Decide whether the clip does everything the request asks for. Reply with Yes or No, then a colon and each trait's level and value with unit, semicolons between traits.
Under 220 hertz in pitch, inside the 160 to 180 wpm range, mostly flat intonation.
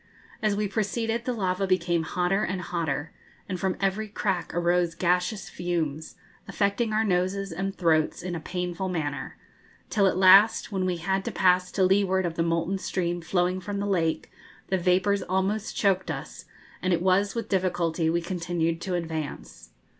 Yes: medium, 185 Hz; average, 170 wpm; narrow, 2.3 semitones